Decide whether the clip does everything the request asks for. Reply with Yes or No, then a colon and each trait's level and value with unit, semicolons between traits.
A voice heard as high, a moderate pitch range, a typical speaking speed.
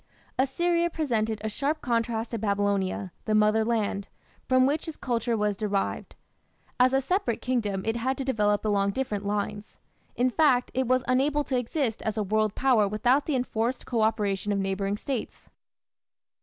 Yes: high, 225 Hz; average, 3.8 semitones; average, 170 wpm